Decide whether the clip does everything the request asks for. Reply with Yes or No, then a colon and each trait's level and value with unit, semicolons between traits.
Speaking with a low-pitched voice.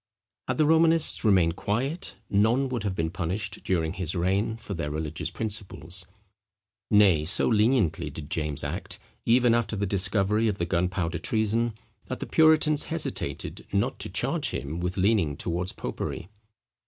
Yes: low, 100 Hz